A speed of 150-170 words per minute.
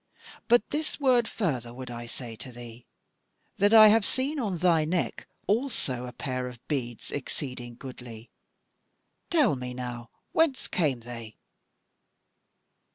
No: slow, 135 wpm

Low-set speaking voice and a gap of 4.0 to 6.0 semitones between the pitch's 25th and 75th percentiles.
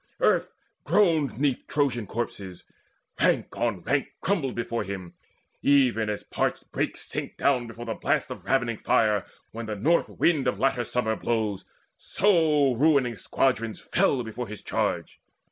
Yes: low, 120 Hz; average, 4.4 semitones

